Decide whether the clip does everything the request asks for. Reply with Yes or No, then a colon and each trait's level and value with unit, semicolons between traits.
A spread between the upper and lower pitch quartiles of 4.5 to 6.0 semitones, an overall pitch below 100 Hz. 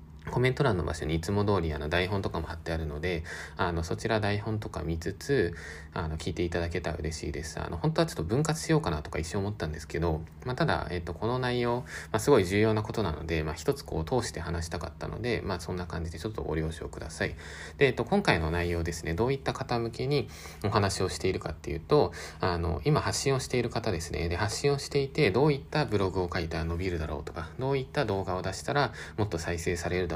Yes: wide, 5.4 semitones; very low, 90 Hz